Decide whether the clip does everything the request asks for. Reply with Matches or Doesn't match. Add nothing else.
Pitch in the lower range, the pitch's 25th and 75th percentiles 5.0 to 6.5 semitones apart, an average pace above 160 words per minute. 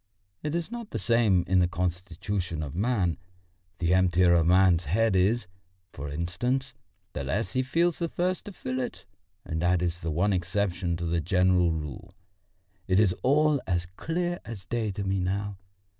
Matches